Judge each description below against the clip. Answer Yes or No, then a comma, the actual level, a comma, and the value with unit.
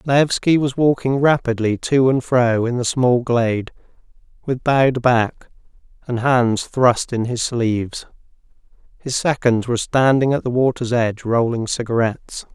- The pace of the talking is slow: No, average, 145 wpm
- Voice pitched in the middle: No, low, 125 Hz